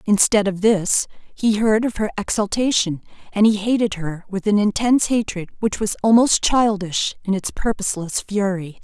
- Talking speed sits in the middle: Yes, average, 165 wpm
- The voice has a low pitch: No, high, 205 Hz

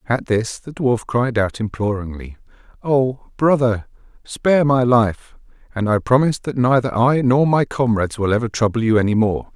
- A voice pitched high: No, low, 120 Hz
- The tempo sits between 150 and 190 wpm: Yes, average, 170 wpm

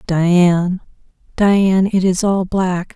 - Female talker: Yes, female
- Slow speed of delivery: Yes, slow, 120 wpm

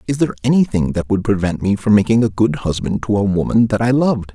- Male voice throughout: Yes, male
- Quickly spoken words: Yes, fast, 250 wpm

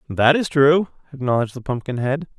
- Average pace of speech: Yes, average, 150 wpm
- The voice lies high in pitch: No, medium, 140 Hz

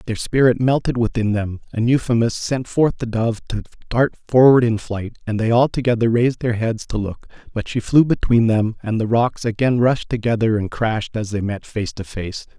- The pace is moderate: No, fast, 210 wpm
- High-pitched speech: No, low, 115 Hz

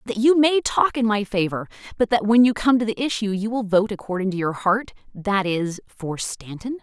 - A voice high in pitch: Yes, high, 215 Hz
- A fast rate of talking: Yes, fast, 230 wpm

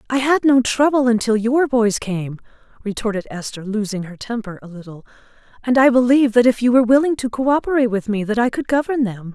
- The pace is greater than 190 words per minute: Yes, fast, 205 wpm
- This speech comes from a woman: Yes, female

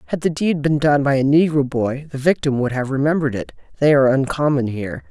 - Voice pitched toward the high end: No, low, 135 Hz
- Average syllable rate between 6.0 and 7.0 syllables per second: Yes, 6.2 syllables/s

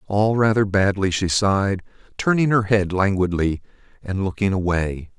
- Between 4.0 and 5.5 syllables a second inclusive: Yes, 4.7 syllables/s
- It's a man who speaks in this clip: Yes, male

